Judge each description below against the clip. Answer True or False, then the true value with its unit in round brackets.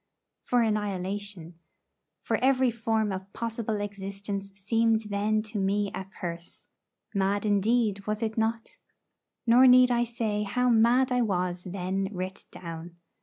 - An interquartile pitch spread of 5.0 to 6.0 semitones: False (3.0 semitones)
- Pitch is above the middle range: True (210 Hz)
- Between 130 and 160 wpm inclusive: True (135 wpm)